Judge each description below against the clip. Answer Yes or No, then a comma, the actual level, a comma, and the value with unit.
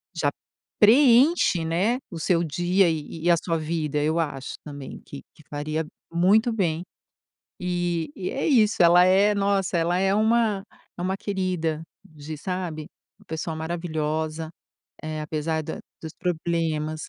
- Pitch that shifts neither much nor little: Yes, average, 3.3 semitones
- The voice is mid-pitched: Yes, medium, 170 Hz